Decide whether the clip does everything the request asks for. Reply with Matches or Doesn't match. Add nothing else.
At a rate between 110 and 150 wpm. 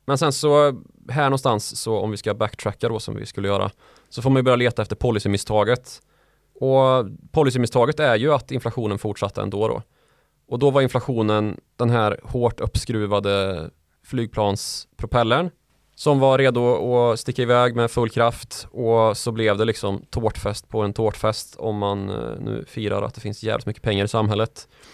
Doesn't match